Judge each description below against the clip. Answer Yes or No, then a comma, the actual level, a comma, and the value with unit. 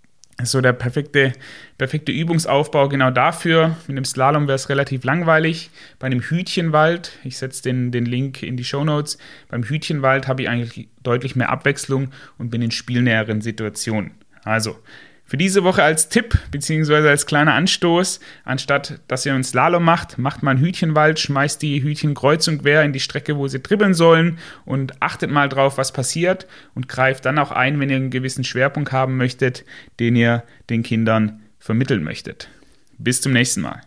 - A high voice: No, low, 135 Hz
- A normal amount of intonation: Yes, average, 3.3 semitones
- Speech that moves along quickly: No, average, 175 wpm